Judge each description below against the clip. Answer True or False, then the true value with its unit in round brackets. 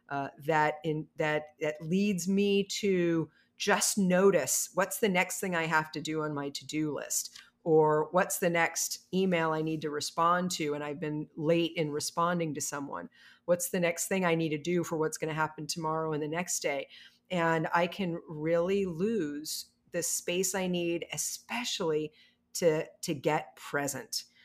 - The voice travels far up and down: False (2.9 semitones)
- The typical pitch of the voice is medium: True (165 Hz)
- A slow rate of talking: False (175 wpm)